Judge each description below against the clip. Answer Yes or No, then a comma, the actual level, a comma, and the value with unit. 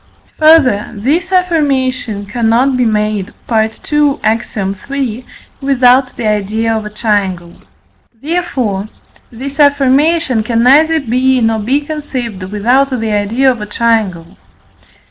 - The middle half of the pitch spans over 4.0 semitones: Yes, average, 4.5 semitones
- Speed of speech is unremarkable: No, slow, 120 wpm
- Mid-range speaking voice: No, high, 240 Hz